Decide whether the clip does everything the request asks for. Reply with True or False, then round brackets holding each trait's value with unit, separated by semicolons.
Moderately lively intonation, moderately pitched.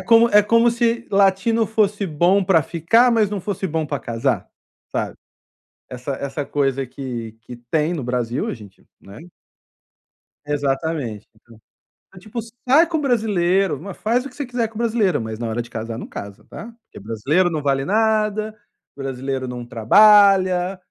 False (8.7 semitones; 175 Hz)